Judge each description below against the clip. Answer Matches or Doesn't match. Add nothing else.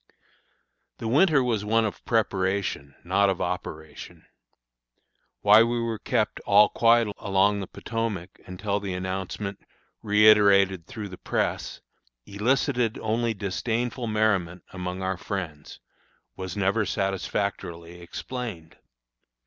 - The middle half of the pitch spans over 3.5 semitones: Doesn't match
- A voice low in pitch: Matches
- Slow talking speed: Matches